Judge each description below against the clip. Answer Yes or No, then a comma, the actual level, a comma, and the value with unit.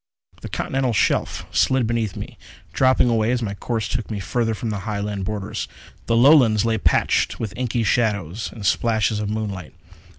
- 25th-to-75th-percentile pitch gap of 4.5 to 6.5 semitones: No, narrow, 2.4 semitones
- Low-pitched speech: Yes, low, 110 Hz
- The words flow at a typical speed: Yes, average, 170 wpm